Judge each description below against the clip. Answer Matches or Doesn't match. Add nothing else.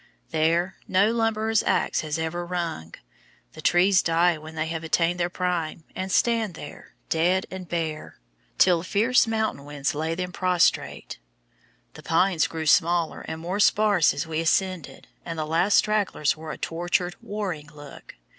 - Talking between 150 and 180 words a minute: Matches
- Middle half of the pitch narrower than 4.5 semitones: Matches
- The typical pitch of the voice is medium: Matches